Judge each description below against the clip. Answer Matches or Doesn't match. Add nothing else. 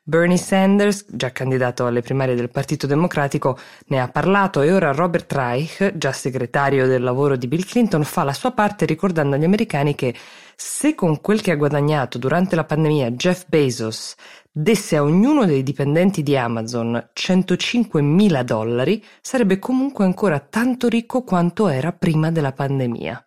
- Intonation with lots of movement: Matches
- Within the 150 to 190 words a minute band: Matches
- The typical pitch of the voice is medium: Matches